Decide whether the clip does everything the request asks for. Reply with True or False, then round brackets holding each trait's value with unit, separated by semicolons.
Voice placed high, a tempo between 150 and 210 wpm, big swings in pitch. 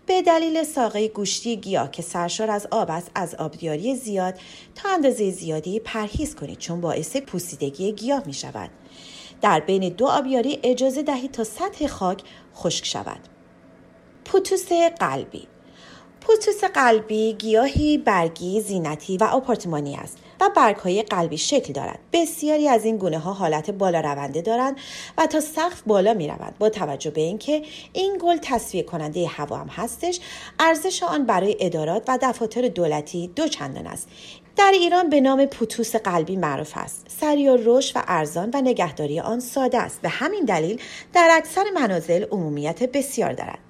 True (225 Hz; 155 wpm; 8.2 semitones)